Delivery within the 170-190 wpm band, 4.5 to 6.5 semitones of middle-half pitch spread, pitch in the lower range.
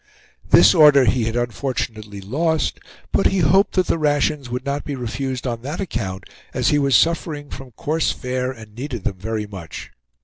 Yes: average, 180 wpm; average, 4.8 semitones; low, 130 Hz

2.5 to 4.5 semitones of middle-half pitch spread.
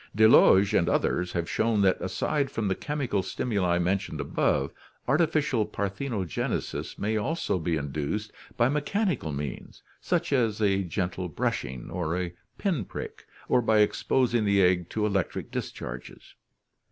No: average, 5.3 semitones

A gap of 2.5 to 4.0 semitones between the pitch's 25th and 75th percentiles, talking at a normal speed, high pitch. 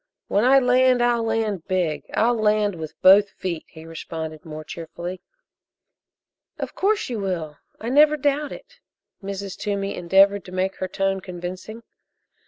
No: average, 4.6 semitones; average, 150 wpm; high, 195 Hz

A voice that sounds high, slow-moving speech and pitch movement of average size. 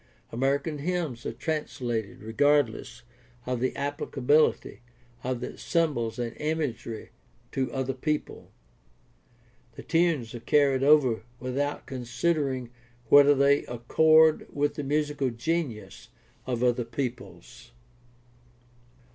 No: low, 135 Hz; slow, 100 wpm; average, 3.4 semitones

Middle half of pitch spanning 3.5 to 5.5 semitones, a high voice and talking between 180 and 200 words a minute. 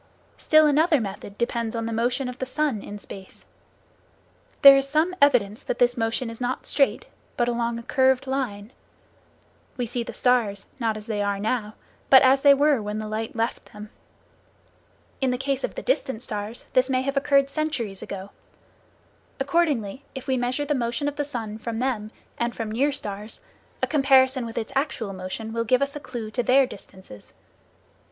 Yes: average, 3.8 semitones; high, 245 Hz; average, 185 wpm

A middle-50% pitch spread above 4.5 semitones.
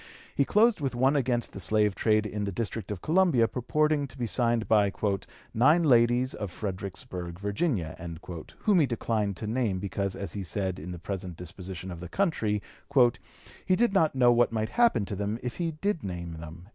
Yes: wide, 5.6 semitones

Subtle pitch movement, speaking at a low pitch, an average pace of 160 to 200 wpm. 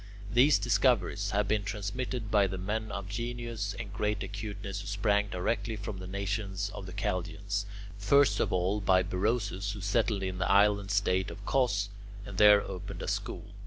Yes: narrow, 1.8 semitones; low, 100 Hz; average, 175 wpm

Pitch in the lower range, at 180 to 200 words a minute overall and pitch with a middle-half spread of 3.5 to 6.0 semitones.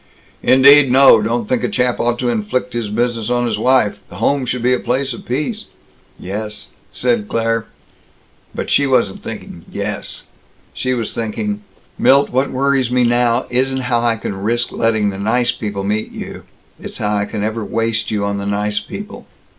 No: low, 120 Hz; average, 185 wpm; average, 3.1 semitones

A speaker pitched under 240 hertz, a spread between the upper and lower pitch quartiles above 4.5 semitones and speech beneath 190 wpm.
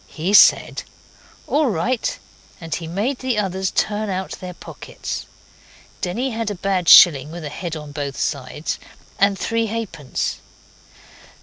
Yes: high, 190 Hz; average, 5.1 semitones; average, 140 wpm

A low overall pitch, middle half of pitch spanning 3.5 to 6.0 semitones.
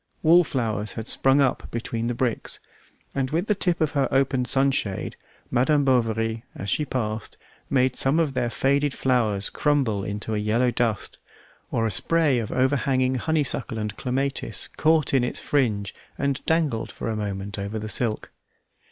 Yes: low, 125 Hz; average, 4.0 semitones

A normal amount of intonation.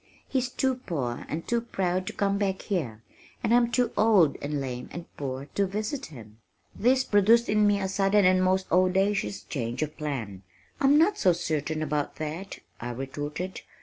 No: wide, 6.1 semitones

